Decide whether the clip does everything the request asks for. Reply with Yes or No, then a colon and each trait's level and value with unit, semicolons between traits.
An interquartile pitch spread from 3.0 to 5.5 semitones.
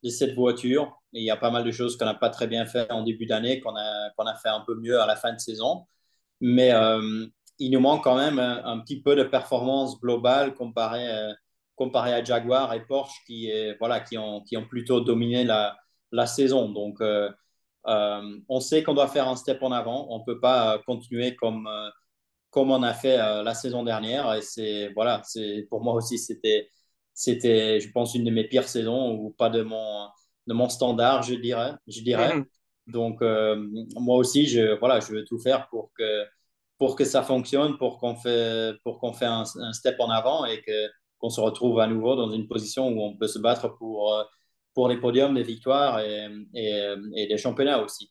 No: narrow, 2.6 semitones